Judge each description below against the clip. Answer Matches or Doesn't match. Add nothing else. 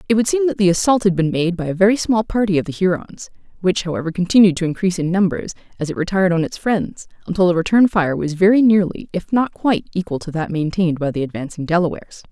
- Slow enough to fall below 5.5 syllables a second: Doesn't match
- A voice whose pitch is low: Doesn't match